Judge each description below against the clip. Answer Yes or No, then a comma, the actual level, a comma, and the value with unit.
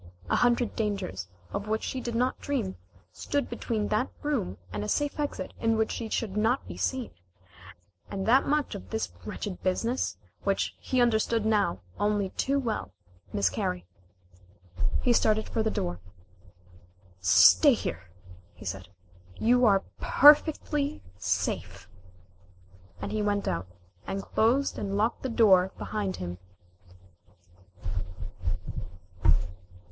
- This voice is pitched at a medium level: No, high, 220 Hz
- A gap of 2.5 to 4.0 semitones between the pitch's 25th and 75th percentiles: No, average, 4.5 semitones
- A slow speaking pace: Yes, slow, 130 wpm